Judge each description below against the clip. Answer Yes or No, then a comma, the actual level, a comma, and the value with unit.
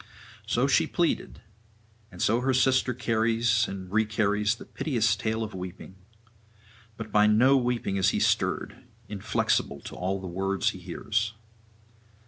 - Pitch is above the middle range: No, low, 105 Hz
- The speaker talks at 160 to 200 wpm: No, average, 140 wpm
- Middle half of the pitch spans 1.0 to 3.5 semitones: Yes, average, 3.1 semitones